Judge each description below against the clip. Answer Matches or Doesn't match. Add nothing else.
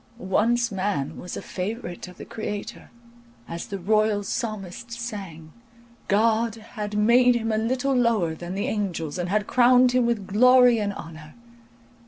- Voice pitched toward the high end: Matches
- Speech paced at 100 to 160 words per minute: Matches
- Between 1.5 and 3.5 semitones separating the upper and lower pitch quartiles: Doesn't match